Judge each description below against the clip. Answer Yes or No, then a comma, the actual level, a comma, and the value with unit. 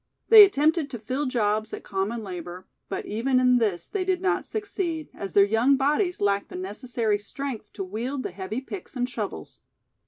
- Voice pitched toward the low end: No, high, 240 Hz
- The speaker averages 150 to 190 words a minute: Yes, average, 185 wpm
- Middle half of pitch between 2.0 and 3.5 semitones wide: No, wide, 5.6 semitones